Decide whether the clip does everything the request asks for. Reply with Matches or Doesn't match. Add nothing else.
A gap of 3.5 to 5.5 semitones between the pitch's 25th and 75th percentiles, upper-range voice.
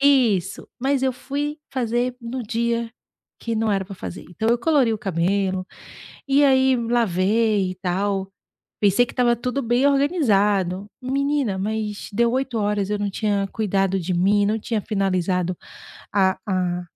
Matches